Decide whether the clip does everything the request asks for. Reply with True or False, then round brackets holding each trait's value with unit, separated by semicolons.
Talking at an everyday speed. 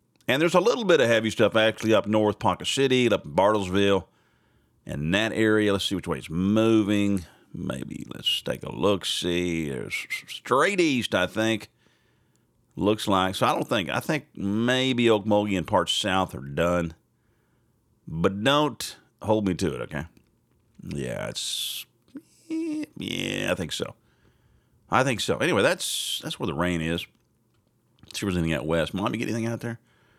True (170 wpm)